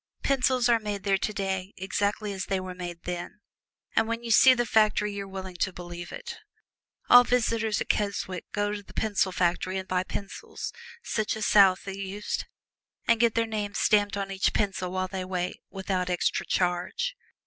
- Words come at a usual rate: Yes, average, 180 wpm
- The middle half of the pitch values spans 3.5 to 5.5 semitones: No, narrow, 2.6 semitones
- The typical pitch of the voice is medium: No, high, 200 Hz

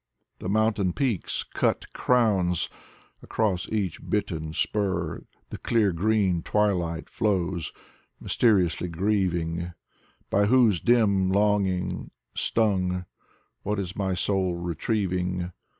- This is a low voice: Yes, very low, 95 Hz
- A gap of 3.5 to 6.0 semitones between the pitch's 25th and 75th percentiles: No, average, 3.0 semitones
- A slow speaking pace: Yes, slow, 100 wpm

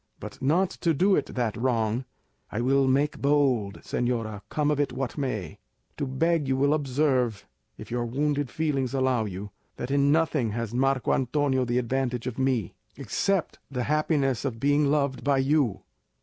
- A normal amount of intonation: Yes, average, 3.1 semitones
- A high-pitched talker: No, low, 135 Hz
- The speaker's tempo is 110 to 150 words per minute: No, average, 170 wpm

